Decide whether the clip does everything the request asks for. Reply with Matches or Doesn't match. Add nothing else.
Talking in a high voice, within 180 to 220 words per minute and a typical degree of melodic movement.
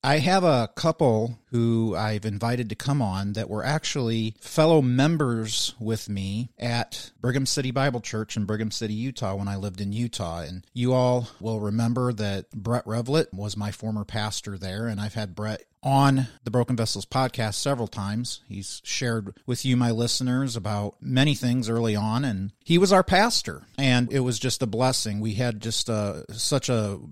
Doesn't match